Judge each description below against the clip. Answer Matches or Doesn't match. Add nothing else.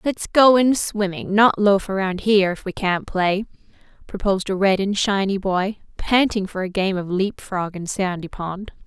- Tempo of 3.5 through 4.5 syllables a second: Matches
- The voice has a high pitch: Matches